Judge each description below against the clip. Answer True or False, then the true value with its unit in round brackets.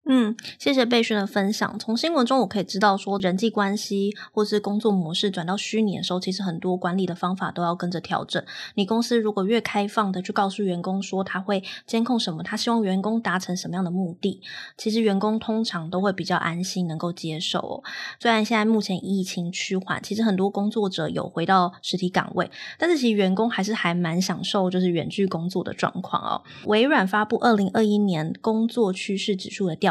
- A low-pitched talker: False (195 Hz)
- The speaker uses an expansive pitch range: False (3.0 semitones)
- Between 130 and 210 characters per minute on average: False (330 characters per minute)